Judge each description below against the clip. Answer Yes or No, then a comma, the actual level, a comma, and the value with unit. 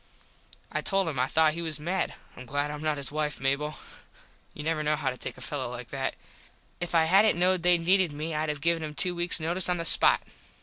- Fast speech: Yes, fast, 235 wpm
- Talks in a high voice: No, medium, 155 Hz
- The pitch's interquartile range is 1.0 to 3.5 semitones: Yes, average, 2.8 semitones